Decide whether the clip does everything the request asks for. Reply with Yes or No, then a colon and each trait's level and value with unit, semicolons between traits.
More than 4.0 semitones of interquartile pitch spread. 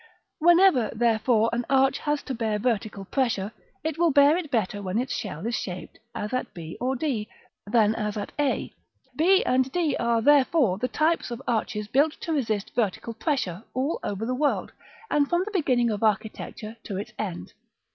Yes: average, 5.2 semitones